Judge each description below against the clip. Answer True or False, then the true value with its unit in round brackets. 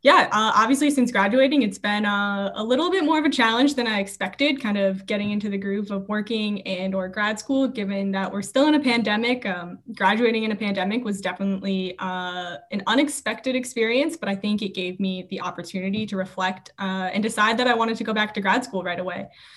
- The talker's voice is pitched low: False (210 Hz)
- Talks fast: True (220 wpm)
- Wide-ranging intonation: False (3.6 semitones)